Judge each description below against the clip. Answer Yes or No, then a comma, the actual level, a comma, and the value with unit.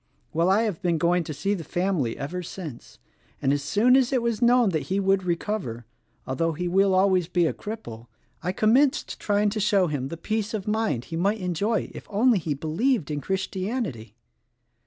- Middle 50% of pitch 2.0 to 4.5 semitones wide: No, average, 4.9 semitones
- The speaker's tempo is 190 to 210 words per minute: Yes, average, 200 wpm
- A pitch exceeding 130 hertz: Yes, high, 190 Hz